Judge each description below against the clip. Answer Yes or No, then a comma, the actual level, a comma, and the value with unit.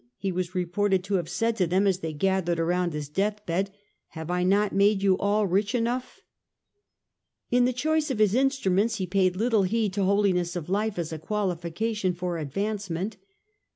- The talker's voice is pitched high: Yes, high, 195 Hz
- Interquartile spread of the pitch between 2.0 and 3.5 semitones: Yes, average, 3.0 semitones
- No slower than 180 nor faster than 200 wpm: Yes, average, 190 wpm